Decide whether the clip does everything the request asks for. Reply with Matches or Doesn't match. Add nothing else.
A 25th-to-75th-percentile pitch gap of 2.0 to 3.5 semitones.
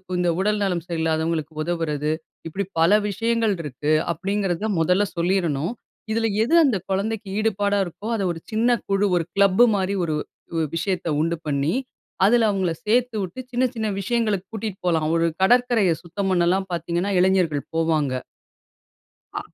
Doesn't match